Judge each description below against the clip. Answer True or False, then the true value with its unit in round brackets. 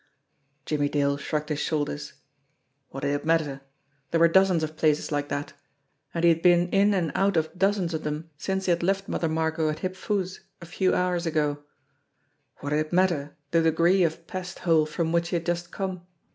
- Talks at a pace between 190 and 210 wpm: True (200 wpm)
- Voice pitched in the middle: True (165 Hz)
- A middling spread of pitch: True (3.0 semitones)